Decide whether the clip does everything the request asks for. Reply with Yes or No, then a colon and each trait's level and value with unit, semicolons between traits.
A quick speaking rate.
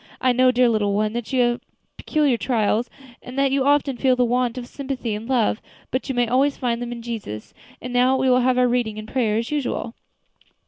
Yes: fast, 225 wpm